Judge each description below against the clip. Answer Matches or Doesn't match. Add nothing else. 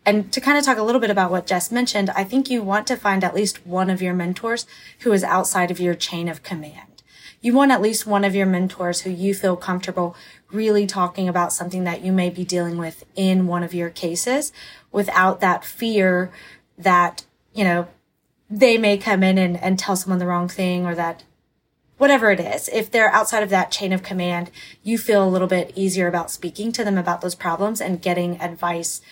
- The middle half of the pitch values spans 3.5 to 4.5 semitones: Doesn't match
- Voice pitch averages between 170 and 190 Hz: Matches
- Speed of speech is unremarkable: Doesn't match